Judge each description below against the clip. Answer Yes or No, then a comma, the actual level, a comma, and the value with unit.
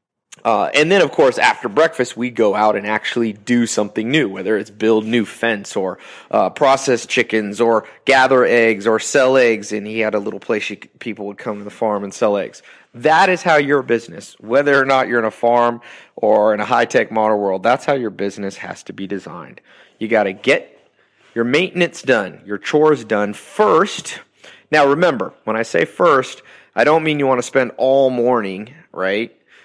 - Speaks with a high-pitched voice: No, low, 115 Hz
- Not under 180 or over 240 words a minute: Yes, average, 200 wpm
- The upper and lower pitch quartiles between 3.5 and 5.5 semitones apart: Yes, average, 4.0 semitones